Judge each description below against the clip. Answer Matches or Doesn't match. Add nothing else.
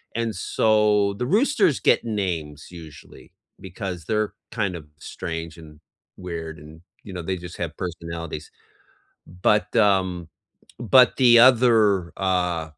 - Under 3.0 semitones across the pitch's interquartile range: Doesn't match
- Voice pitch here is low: Matches